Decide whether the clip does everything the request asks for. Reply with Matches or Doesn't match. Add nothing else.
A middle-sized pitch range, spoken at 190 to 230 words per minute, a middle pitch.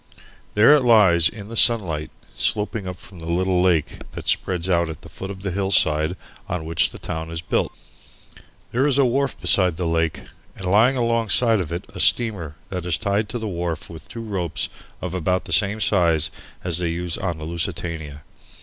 Doesn't match